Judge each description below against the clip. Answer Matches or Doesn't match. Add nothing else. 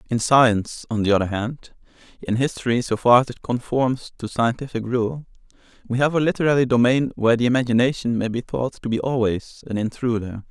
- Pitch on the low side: Matches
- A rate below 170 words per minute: Doesn't match